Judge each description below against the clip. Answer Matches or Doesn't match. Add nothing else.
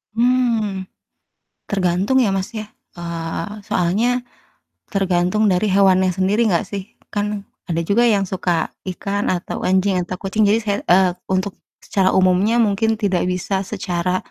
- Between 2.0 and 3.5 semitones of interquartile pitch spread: Matches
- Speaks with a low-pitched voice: Doesn't match